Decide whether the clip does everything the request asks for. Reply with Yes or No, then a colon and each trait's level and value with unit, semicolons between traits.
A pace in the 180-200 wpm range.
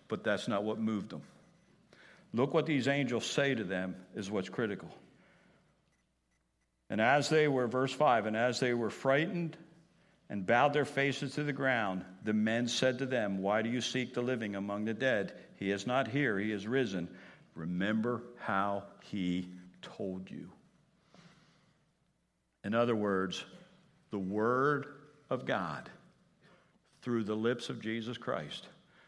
No: average, 150 wpm